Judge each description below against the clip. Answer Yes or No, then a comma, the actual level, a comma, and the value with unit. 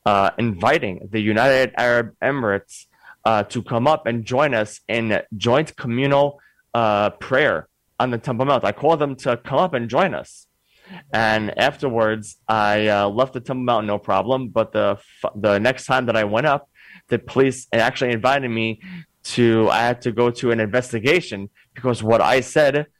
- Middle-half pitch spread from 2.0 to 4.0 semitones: Yes, average, 3.1 semitones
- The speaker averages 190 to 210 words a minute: No, average, 175 wpm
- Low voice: Yes, low, 115 Hz